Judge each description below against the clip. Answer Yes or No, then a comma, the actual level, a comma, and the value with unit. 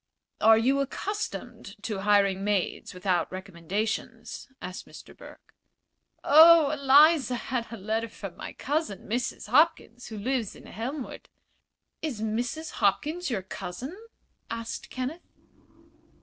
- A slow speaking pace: Yes, slow, 120 wpm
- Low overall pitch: No, high, 230 Hz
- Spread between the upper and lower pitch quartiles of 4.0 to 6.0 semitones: Yes, wide, 5.6 semitones